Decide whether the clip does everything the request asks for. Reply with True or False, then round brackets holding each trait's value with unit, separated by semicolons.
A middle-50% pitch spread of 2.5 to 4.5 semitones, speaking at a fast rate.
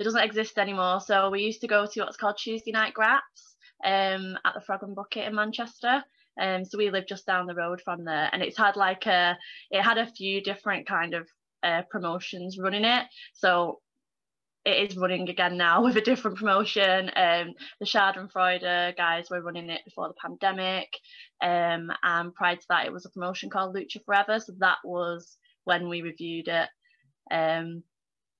False (3.3 semitones; 190 wpm)